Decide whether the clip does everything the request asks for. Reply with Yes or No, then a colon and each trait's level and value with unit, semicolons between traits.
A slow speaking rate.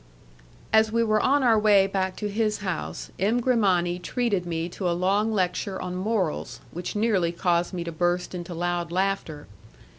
No: average, 175 wpm